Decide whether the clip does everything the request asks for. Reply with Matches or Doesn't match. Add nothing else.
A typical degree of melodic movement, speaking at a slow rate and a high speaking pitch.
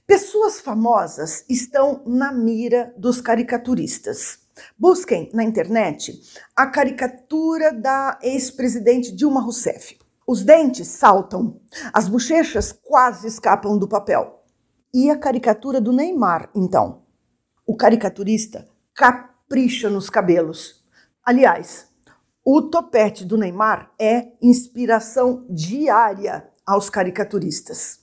Matches